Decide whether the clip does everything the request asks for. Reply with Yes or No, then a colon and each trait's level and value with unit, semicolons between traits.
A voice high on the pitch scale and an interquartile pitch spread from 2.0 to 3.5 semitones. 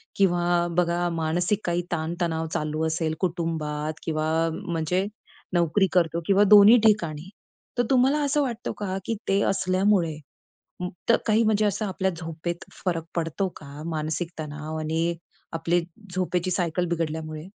No: medium, 175 Hz; average, 3.2 semitones